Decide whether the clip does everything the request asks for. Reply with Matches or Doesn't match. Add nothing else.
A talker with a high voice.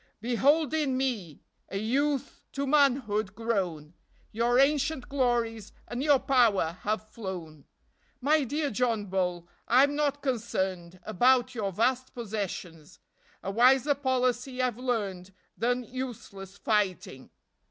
Matches